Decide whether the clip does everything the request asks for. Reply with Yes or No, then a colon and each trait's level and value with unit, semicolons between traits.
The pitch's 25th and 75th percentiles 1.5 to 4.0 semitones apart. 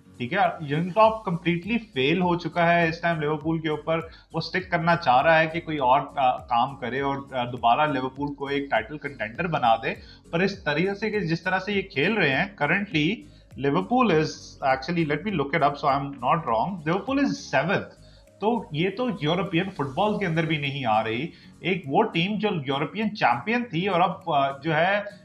No: average, 5.1 semitones